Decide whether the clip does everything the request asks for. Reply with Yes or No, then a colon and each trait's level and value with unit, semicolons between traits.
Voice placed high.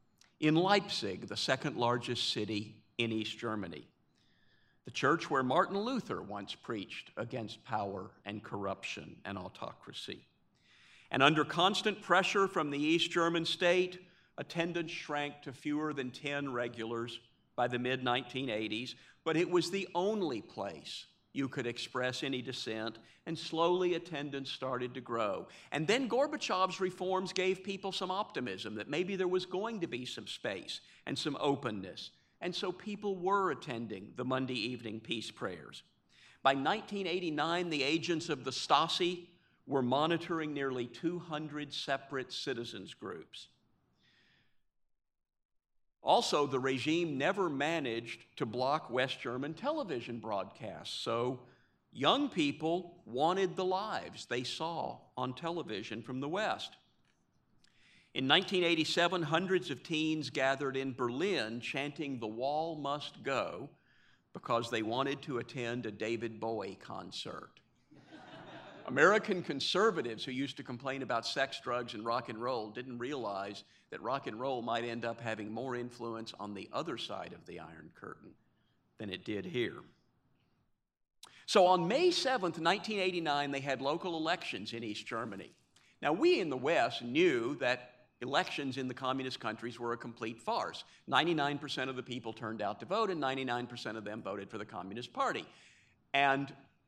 No: low, 135 Hz